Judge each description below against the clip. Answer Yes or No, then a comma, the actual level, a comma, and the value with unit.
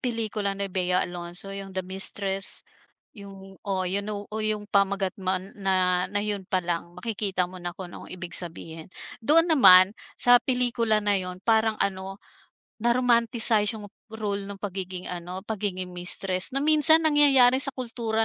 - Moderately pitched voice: No, high, 200 Hz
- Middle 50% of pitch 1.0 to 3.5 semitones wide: Yes, average, 3.1 semitones